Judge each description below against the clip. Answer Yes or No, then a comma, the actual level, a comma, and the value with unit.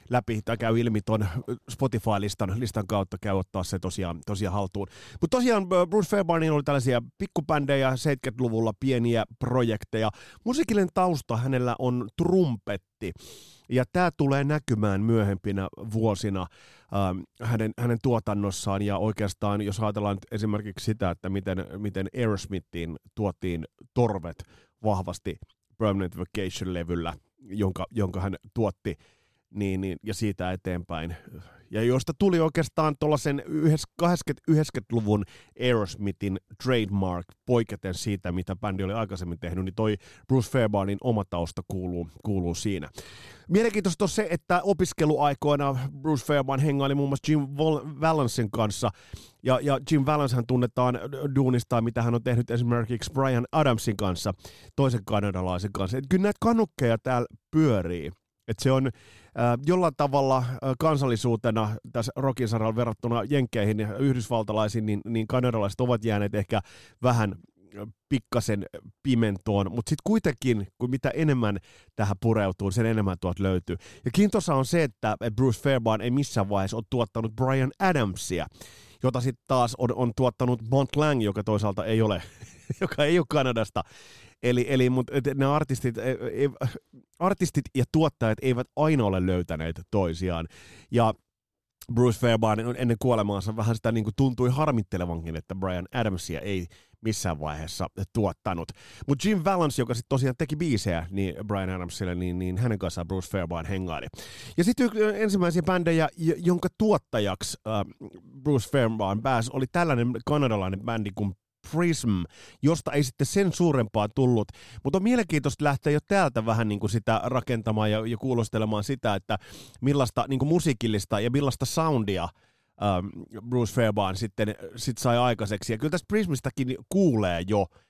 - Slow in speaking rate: No, average, 140 wpm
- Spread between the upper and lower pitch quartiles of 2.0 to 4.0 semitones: No, average, 5.2 semitones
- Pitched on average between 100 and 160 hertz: Yes, low, 115 Hz